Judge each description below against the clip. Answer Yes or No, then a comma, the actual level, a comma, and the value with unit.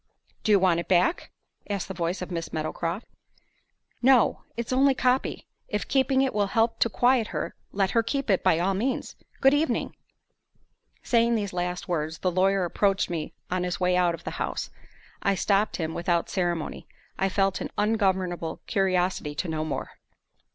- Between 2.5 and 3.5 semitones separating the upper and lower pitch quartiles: No, average, 4.3 semitones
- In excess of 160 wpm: Yes, average, 180 wpm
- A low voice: No, high, 190 Hz